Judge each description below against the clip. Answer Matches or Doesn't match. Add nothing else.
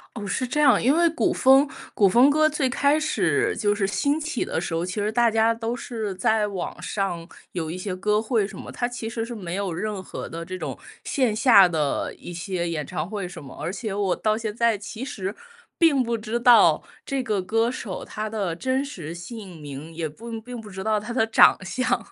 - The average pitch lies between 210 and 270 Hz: Matches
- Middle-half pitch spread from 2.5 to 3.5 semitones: Doesn't match